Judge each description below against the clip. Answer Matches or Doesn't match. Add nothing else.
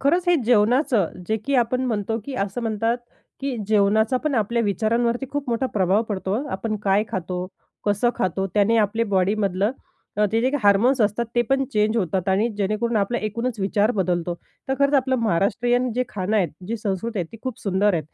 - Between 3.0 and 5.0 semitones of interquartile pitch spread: Matches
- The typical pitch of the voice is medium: Doesn't match